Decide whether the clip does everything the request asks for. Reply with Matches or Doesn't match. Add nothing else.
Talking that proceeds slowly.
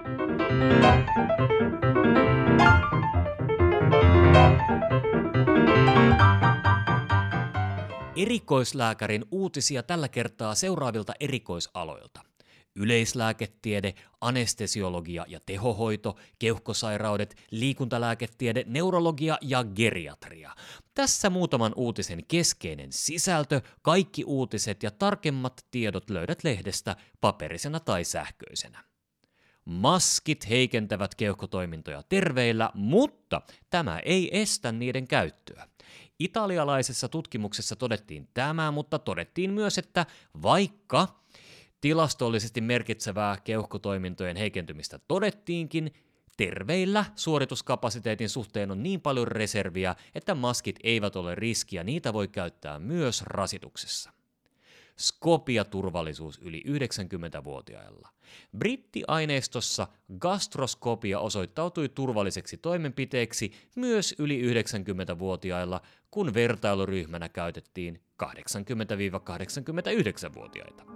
Matches